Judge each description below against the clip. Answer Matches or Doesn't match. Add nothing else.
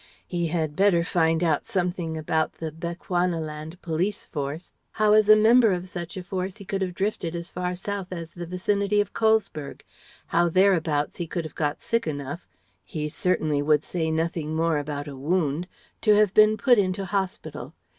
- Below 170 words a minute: Doesn't match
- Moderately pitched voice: Matches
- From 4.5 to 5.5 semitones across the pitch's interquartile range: Doesn't match